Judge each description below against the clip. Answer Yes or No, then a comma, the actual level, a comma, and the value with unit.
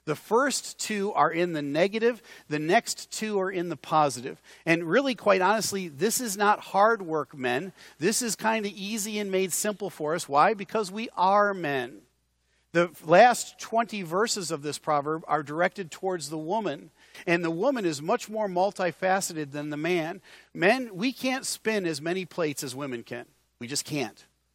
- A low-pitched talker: No, medium, 185 Hz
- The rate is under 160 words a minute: No, average, 180 wpm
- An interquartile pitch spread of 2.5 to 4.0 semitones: No, wide, 5.4 semitones